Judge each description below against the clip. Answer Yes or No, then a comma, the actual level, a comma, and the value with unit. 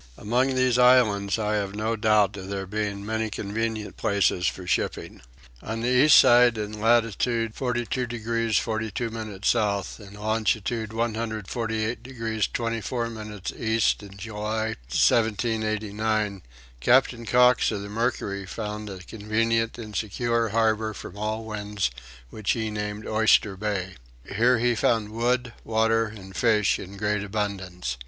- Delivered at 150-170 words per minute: No, average, 140 wpm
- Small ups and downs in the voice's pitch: Yes, narrow, 1.9 semitones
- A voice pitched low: Yes, low, 110 Hz